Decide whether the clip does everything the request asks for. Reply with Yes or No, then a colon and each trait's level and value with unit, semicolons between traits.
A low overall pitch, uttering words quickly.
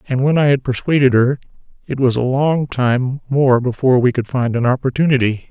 No: low, 130 Hz; average, 195 wpm